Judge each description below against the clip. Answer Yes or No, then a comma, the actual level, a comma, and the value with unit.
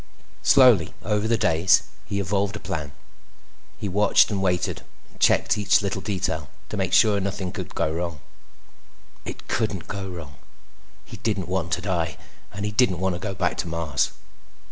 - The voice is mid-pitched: No, very low, 95 Hz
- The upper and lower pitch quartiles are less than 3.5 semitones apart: Yes, average, 3.1 semitones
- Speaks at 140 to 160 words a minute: No, average, 170 wpm